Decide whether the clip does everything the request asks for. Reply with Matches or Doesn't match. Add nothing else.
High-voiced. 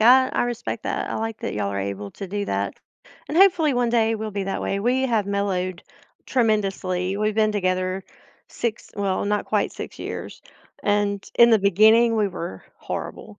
Matches